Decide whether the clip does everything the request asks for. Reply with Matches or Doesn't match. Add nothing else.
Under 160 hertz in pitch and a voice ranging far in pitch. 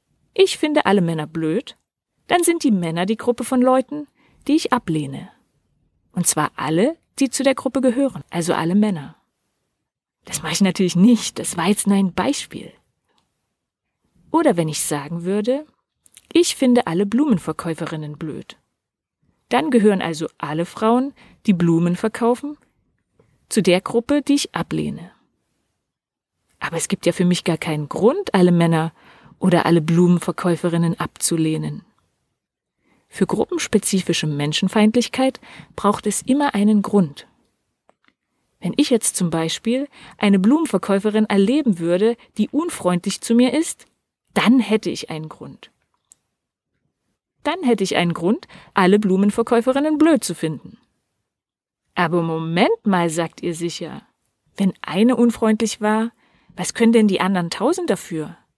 Doesn't match